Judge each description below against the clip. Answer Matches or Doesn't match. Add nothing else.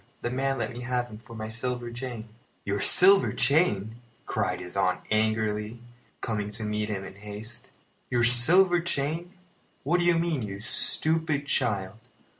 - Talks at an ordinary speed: Matches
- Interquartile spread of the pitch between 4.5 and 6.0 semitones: Matches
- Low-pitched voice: Matches